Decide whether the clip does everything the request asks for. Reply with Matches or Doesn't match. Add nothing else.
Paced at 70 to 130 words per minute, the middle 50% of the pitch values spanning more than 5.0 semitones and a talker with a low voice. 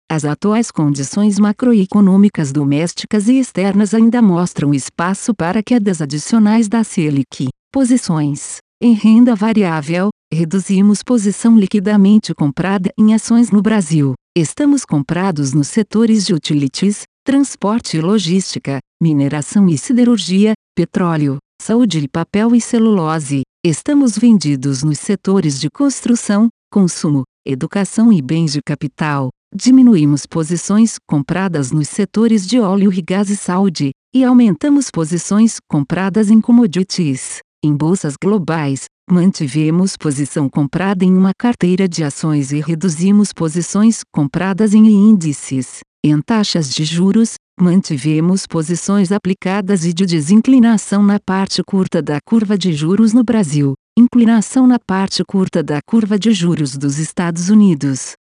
Doesn't match